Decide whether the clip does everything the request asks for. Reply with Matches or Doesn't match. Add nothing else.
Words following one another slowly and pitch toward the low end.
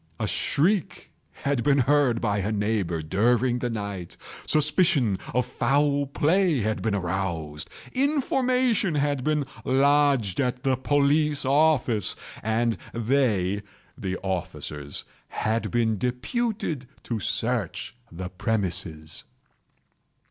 Matches